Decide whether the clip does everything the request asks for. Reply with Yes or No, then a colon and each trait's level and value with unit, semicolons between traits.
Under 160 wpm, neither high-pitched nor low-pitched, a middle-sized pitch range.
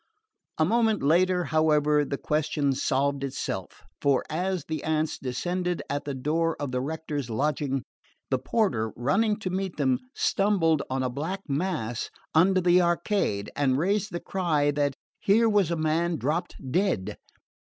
Yes: average, 150 wpm; medium, 155 Hz; average, 4.6 semitones